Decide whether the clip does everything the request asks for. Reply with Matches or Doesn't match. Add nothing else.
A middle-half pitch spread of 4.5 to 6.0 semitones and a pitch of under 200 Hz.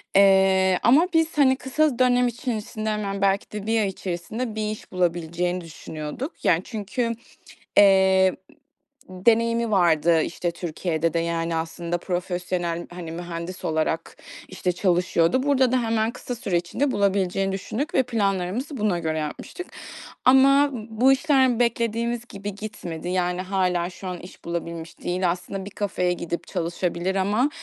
Matches